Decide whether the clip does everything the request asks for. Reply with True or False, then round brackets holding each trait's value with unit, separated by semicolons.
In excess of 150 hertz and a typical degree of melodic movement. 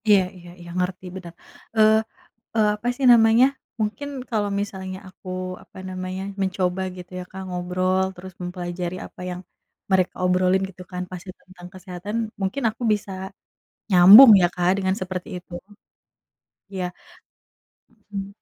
False (185 Hz; 2.0 semitones)